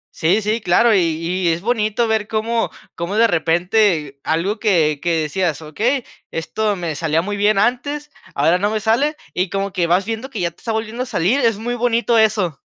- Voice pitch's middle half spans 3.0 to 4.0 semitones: No, average, 4.9 semitones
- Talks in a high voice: Yes, high, 205 Hz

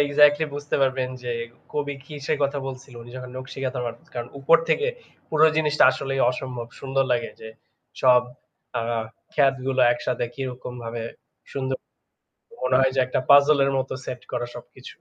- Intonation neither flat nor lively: No, narrow, 2.3 semitones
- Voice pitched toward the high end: No, low, 130 Hz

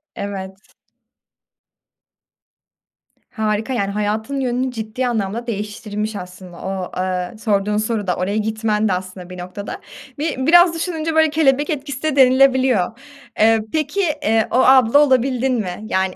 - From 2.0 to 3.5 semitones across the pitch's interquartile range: No, average, 4.8 semitones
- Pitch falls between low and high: No, high, 220 Hz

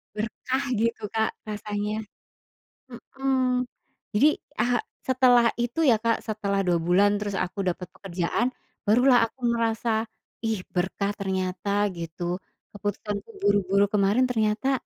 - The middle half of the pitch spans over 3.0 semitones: Yes, average, 3.4 semitones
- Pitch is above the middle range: Yes, high, 215 Hz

